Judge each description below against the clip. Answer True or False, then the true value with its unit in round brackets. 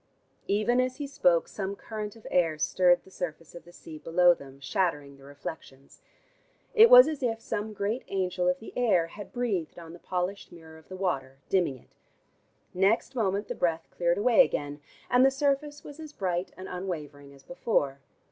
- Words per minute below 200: True (185 wpm)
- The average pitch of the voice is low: False (180 Hz)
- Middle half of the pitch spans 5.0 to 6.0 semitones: True (5.4 semitones)